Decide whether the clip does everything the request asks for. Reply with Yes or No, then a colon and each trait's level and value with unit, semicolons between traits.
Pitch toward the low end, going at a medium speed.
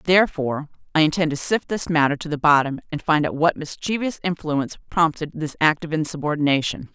No: medium, 155 Hz; average, 180 wpm